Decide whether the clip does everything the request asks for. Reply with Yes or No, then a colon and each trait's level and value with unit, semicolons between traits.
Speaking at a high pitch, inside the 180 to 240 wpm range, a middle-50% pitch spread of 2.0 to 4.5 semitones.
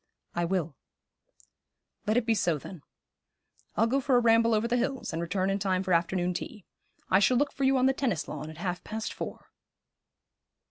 No: high, 205 Hz; average, 195 wpm; wide, 5.5 semitones